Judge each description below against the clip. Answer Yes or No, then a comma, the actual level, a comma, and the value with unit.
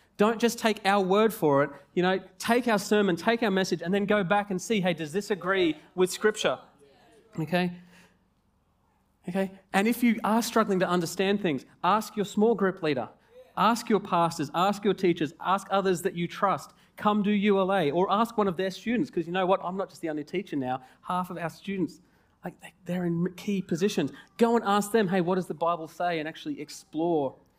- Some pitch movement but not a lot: Yes, average, 3.2 semitones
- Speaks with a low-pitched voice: No, high, 190 Hz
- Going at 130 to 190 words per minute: No, fast, 205 wpm